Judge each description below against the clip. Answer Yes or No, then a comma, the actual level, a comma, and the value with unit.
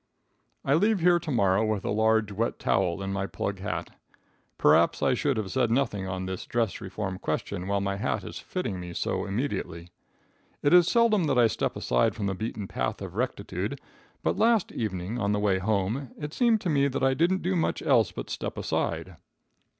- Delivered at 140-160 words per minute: No, average, 200 wpm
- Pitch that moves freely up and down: Yes, wide, 6.9 semitones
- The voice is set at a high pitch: No, low, 110 Hz